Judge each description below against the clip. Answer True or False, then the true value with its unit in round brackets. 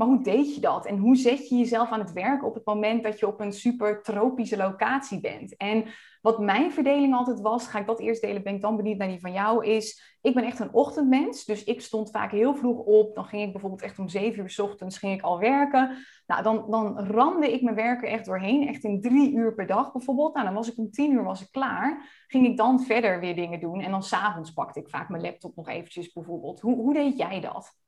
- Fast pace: True (255 wpm)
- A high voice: True (220 Hz)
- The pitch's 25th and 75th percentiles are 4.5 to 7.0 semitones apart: False (3.8 semitones)